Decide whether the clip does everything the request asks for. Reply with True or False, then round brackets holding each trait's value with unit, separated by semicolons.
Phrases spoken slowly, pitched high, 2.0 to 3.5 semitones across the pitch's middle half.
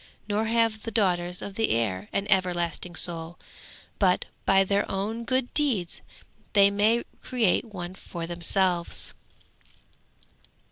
False (125 wpm; 195 Hz; 3.9 semitones)